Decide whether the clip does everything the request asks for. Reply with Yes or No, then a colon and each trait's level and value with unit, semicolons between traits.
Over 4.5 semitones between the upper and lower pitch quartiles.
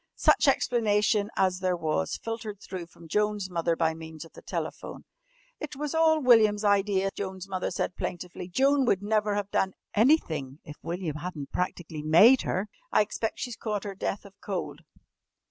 No: average, 3.8 semitones